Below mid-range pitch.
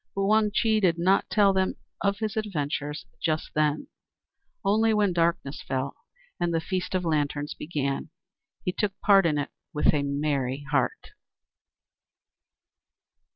No: medium, 170 Hz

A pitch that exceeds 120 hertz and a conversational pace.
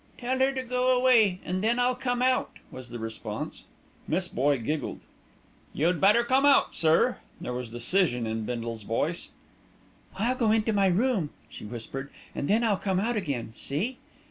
Yes: high, 190 Hz; average, 170 wpm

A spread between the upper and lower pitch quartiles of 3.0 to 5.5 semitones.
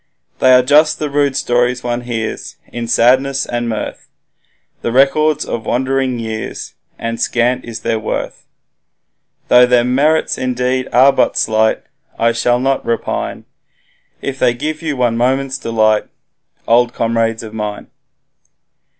No: narrow, 2.4 semitones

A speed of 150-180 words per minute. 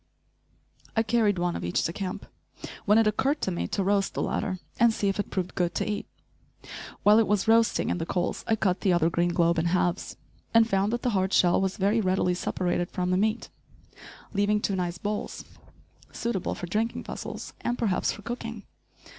No: average, 200 wpm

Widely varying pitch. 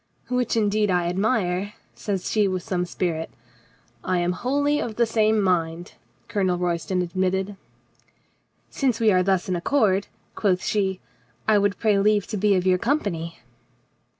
No: average, 3.1 semitones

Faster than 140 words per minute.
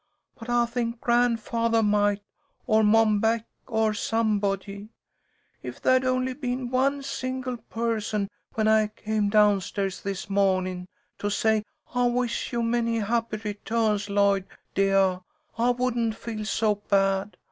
No: slow, 135 wpm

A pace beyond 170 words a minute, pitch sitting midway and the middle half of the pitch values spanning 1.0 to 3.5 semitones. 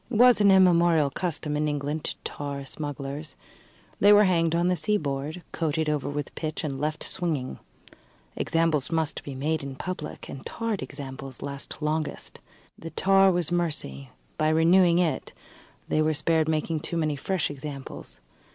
No: average, 160 wpm; medium, 155 Hz; average, 3.2 semitones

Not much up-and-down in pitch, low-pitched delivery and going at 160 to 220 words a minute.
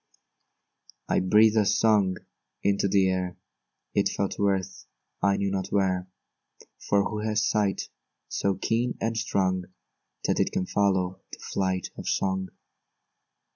No: narrow, 1.9 semitones; low, 100 Hz; slow, 135 wpm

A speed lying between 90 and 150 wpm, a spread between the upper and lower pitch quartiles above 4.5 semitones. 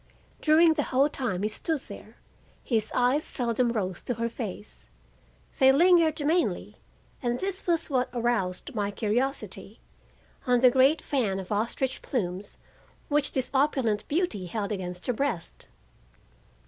Yes: slow, 135 wpm; wide, 5.4 semitones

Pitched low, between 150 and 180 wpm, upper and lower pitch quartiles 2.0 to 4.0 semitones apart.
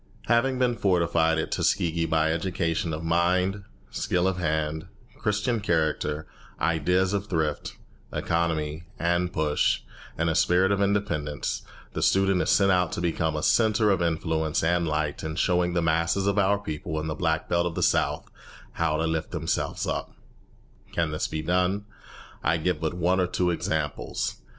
Yes: very low, 85 Hz; average, 165 wpm; average, 2.9 semitones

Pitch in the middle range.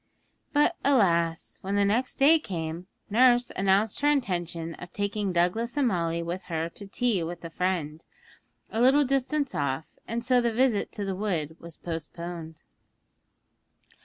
No: high, 195 Hz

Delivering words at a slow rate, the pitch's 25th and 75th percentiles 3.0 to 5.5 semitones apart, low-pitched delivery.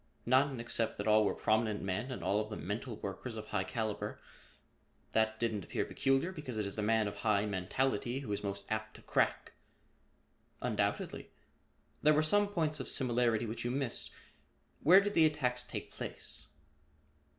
No: average, 175 wpm; average, 4.1 semitones; low, 115 Hz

